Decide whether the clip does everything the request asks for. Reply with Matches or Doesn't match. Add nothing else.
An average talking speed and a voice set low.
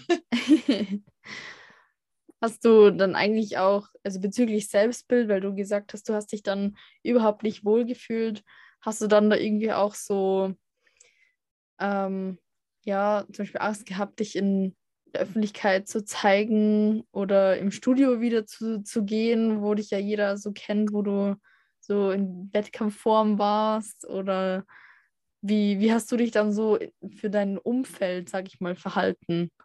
Doesn't match